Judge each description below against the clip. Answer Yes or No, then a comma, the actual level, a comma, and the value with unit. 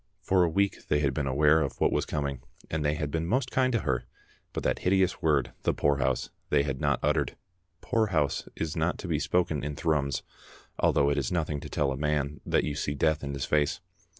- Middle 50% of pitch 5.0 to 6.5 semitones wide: No, average, 2.7 semitones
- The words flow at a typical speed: No, fast, 220 wpm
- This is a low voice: Yes, very low, 75 Hz